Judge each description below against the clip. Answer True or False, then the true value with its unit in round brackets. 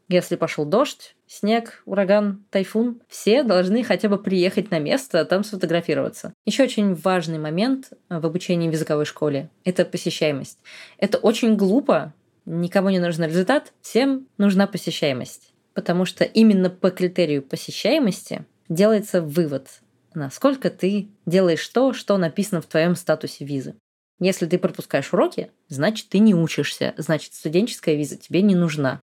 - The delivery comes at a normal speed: True (140 wpm)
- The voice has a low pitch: False (185 Hz)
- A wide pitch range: False (4.0 semitones)